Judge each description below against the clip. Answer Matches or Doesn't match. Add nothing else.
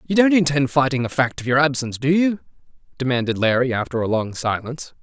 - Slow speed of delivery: Doesn't match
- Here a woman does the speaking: Doesn't match